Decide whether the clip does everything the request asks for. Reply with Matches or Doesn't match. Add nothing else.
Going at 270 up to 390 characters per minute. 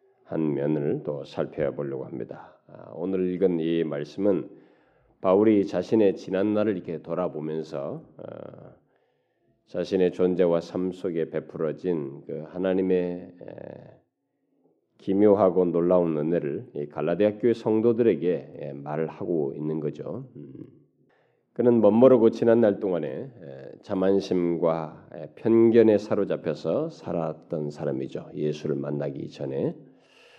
Doesn't match